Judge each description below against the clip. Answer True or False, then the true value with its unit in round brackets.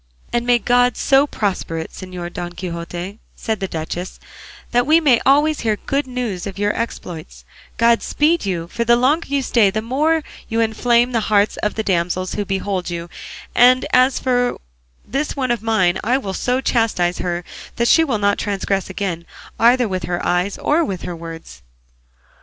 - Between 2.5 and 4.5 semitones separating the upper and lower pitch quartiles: False (5.4 semitones)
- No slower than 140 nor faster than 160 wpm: False (180 wpm)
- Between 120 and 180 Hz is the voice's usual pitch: False (220 Hz)